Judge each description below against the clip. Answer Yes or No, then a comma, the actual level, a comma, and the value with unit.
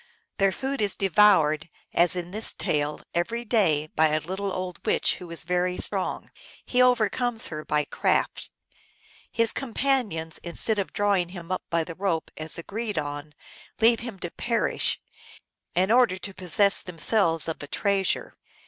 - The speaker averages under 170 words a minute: Yes, average, 160 wpm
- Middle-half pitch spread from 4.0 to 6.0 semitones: Yes, average, 4.7 semitones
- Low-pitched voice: No, medium, 185 Hz